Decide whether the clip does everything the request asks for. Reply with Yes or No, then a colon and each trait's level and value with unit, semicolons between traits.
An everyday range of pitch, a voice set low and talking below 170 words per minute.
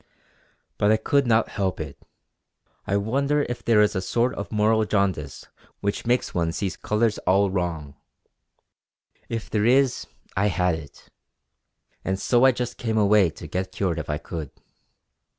Yes: average, 4.1 semitones; low, 100 Hz; average, 160 wpm